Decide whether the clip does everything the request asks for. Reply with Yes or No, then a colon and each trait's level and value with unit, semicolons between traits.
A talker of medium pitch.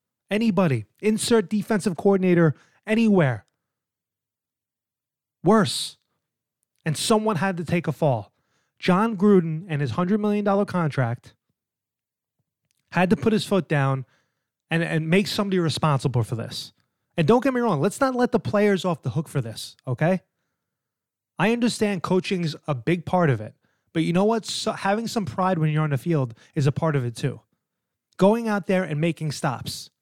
Yes: medium, 170 Hz